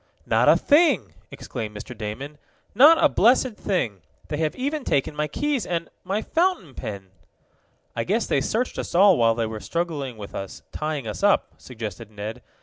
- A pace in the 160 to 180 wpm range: Yes, average, 175 wpm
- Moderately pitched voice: Yes, medium, 150 Hz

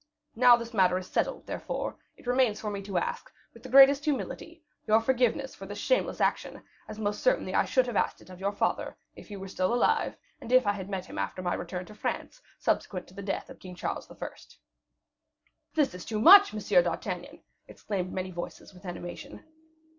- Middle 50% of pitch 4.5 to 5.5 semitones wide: Yes, average, 5.2 semitones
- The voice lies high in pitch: Yes, high, 205 Hz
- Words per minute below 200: No, fast, 205 wpm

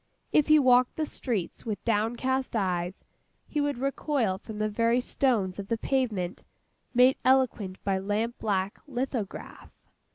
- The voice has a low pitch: No, high, 230 Hz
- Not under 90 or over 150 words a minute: Yes, average, 140 wpm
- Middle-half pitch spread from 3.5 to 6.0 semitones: Yes, average, 4.6 semitones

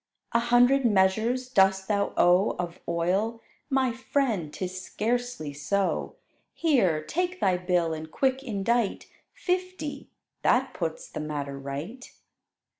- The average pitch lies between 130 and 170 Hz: No, high, 205 Hz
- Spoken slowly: Yes, slow, 120 wpm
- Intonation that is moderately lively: No, wide, 6.3 semitones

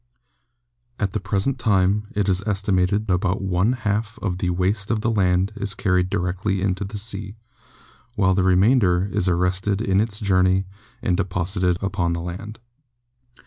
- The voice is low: Yes, very low, 95 Hz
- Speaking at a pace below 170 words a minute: Yes, average, 160 wpm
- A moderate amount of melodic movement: No, narrow, 2.1 semitones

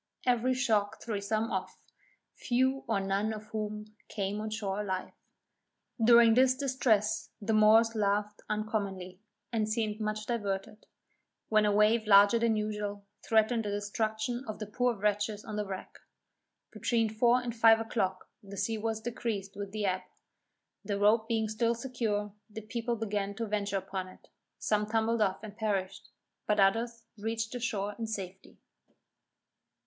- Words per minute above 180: No, average, 155 wpm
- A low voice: No, high, 215 Hz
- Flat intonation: Yes, narrow, 1.9 semitones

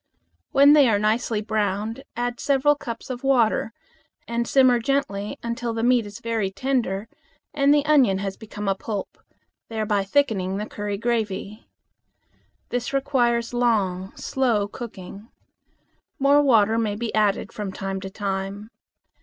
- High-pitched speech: Yes, high, 225 Hz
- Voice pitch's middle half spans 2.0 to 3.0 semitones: No, average, 3.4 semitones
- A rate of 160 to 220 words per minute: No, average, 140 wpm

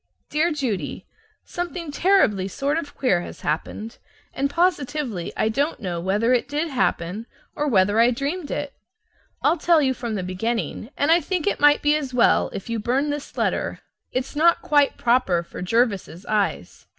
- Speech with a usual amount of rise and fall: No, wide, 6.1 semitones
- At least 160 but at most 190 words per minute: Yes, average, 175 wpm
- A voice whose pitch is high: Yes, very high, 255 Hz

